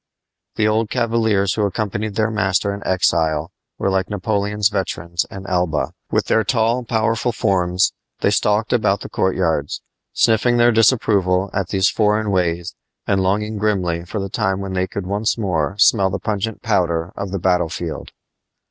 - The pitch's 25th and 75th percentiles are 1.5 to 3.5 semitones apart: Yes, average, 2.9 semitones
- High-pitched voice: No, low, 100 Hz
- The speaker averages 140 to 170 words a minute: Yes, average, 165 wpm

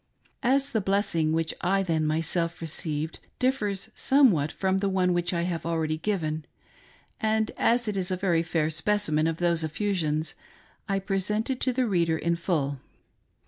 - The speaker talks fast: No, average, 175 wpm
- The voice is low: No, medium, 175 Hz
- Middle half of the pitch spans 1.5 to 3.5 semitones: No, average, 4.2 semitones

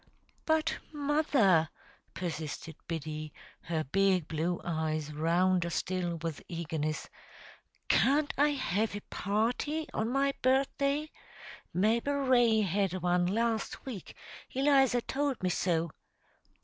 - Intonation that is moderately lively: No, wide, 8.2 semitones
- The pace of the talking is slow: Yes, slow, 110 wpm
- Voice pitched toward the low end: No, high, 195 Hz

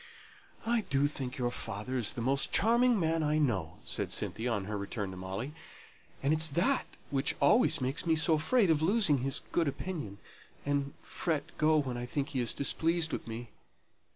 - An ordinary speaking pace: Yes, average, 185 wpm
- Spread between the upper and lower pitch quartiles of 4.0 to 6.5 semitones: Yes, average, 5.0 semitones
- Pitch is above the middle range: No, medium, 140 Hz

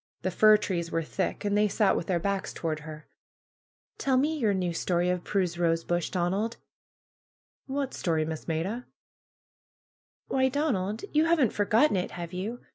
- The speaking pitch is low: No, high, 190 Hz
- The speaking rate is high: No, average, 175 wpm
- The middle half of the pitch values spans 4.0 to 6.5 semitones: Yes, average, 4.9 semitones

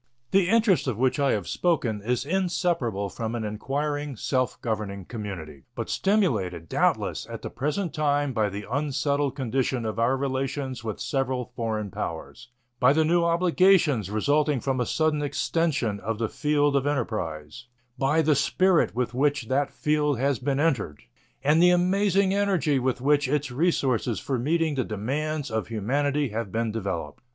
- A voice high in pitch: No, low, 135 Hz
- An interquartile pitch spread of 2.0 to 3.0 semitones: No, average, 5.1 semitones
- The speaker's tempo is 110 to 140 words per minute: No, average, 160 wpm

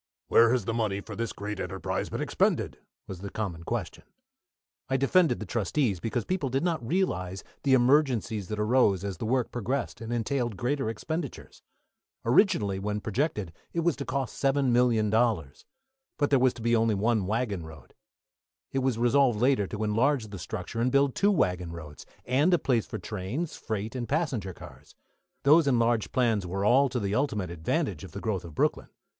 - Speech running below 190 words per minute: Yes, average, 180 wpm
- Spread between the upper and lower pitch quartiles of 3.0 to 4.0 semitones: No, average, 4.8 semitones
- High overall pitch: No, low, 115 Hz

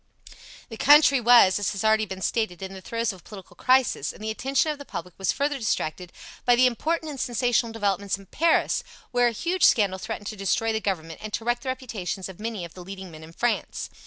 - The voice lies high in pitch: Yes, high, 220 Hz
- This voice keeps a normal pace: No, fast, 230 wpm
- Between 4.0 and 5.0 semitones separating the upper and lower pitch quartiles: Yes, average, 4.4 semitones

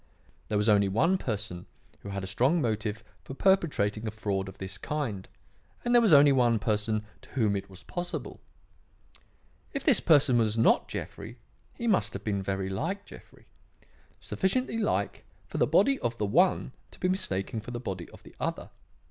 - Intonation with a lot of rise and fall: Yes, wide, 8.8 semitones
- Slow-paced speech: No, average, 180 wpm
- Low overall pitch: Yes, low, 115 Hz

